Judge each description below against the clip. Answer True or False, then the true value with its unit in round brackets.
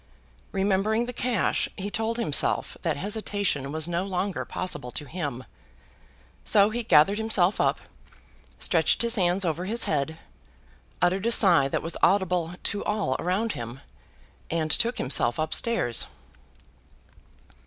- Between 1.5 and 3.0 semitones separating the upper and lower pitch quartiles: False (5.3 semitones)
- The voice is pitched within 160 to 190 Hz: True (185 Hz)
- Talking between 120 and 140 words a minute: True (135 wpm)